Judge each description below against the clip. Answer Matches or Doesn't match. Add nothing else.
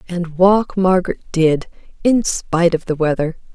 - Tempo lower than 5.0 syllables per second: Matches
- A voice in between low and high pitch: Matches